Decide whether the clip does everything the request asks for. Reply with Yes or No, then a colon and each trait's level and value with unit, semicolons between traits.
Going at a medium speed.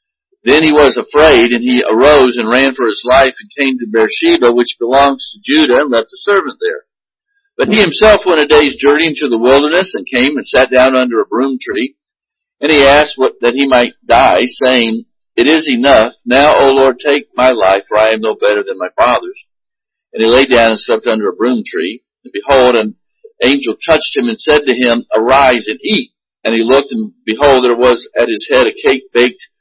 No: fast, 215 wpm